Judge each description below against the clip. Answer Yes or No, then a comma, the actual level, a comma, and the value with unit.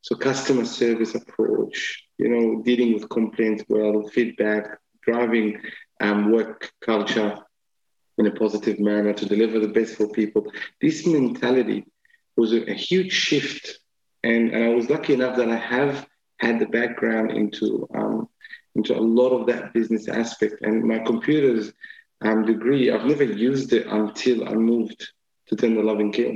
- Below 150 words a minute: No, average, 155 wpm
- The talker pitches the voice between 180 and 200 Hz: No, low, 115 Hz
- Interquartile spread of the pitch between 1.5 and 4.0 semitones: Yes, average, 2.7 semitones